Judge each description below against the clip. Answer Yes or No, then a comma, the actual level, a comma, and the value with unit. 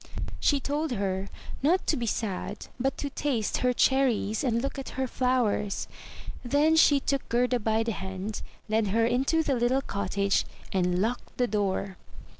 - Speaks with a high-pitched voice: Yes, high, 240 Hz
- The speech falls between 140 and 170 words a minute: Yes, average, 165 wpm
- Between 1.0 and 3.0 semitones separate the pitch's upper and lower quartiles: No, average, 4.8 semitones